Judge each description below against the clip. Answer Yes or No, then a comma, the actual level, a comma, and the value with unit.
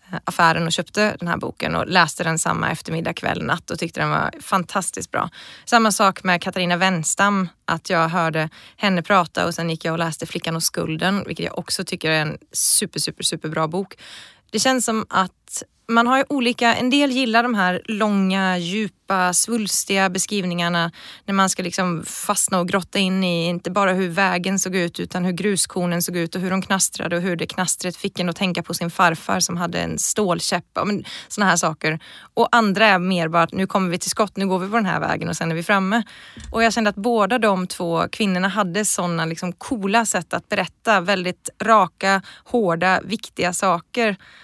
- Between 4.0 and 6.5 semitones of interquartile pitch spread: No, average, 3.2 semitones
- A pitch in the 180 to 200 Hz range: Yes, high, 190 Hz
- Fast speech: Yes, fast, 205 wpm